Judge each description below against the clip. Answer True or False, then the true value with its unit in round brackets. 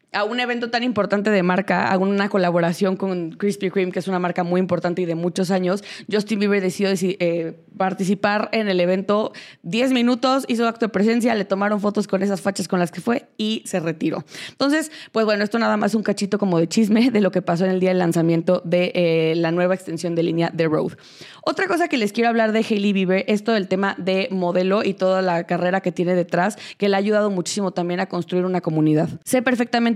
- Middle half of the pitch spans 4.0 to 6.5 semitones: False (3.1 semitones)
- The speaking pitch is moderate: False (195 Hz)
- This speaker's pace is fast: True (225 wpm)